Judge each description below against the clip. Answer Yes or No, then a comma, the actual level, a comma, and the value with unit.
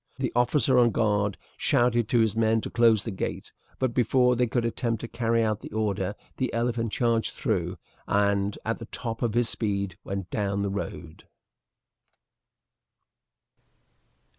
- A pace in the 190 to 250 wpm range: No, average, 155 wpm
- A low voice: Yes, low, 115 Hz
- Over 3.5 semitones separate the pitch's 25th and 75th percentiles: No, average, 2.8 semitones